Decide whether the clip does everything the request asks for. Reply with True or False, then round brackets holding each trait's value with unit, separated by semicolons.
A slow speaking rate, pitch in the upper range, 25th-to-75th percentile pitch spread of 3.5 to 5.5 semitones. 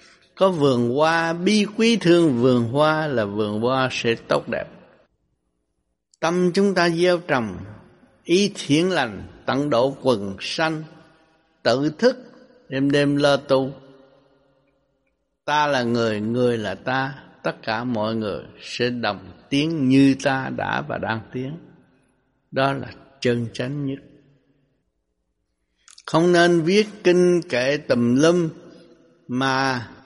False (130 wpm; 135 Hz; 5.1 semitones)